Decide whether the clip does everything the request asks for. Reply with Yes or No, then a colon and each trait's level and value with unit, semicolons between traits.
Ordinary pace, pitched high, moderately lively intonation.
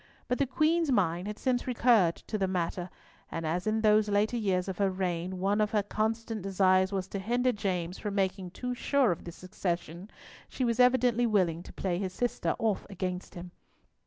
Yes: average, 195 wpm; high, 200 Hz; average, 3.9 semitones